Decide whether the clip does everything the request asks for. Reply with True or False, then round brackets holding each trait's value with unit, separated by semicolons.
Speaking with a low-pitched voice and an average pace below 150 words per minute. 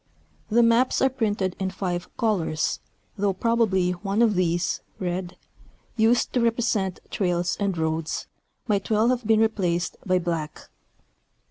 False (195 Hz; 135 wpm)